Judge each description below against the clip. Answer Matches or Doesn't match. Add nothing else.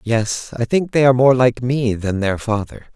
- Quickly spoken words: Matches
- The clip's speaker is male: Matches